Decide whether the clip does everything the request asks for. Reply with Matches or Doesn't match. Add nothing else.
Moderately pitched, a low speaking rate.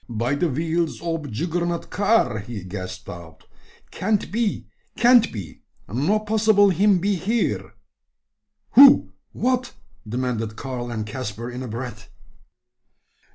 Matches